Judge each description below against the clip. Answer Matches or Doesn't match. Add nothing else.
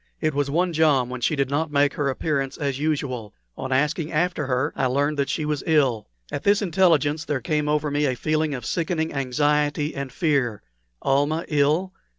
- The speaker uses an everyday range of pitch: Doesn't match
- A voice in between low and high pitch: Matches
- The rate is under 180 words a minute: Doesn't match